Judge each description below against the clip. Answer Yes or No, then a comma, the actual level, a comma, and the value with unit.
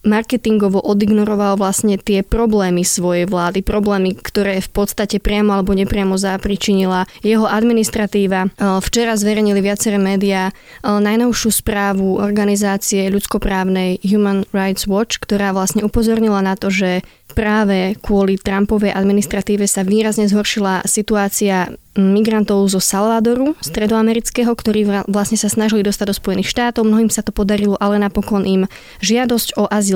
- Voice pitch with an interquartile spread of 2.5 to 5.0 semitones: No, narrow, 1.7 semitones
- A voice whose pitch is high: Yes, high, 205 Hz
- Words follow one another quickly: No, average, 130 wpm